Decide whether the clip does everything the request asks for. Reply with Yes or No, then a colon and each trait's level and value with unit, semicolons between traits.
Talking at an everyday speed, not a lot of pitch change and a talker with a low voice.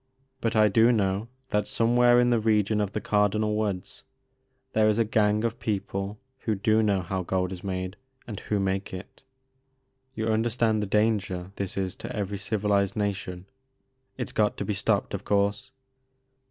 Yes: average, 175 wpm; narrow, 2.0 semitones; low, 105 Hz